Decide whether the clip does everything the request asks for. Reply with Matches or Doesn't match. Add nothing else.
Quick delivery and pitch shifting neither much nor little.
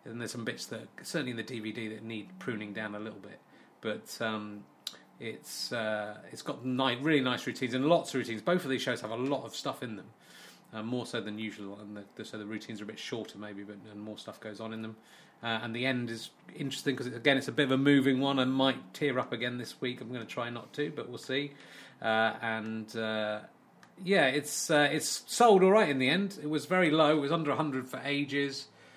Matches